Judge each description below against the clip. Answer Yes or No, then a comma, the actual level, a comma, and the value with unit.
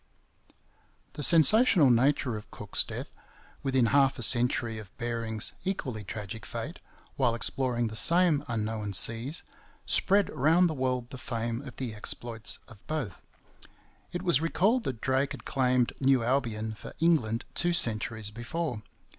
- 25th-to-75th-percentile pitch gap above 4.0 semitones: Yes, average, 4.4 semitones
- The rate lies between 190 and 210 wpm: No, average, 145 wpm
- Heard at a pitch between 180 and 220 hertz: No, low, 125 Hz